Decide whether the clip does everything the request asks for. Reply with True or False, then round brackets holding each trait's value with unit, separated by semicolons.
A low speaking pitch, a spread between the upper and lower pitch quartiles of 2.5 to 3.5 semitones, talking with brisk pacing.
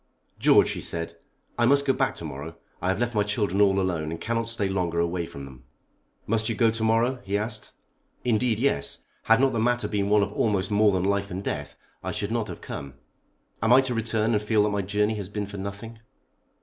True (105 Hz; 3.1 semitones; 225 wpm)